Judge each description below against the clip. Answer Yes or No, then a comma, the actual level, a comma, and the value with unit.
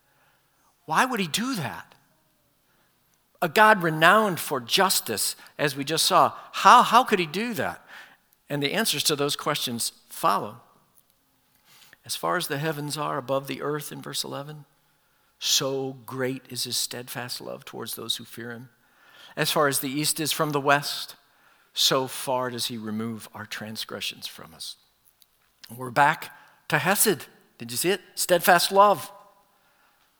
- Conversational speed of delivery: Yes, average, 155 wpm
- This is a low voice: No, medium, 145 Hz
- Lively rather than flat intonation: Yes, wide, 5.9 semitones